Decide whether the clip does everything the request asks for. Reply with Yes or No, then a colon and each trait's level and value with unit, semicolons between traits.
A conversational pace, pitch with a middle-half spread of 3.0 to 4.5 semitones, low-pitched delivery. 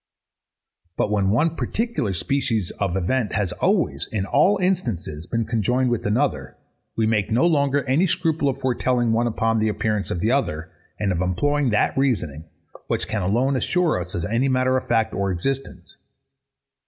No: average, 170 wpm; average, 5.2 semitones; low, 115 Hz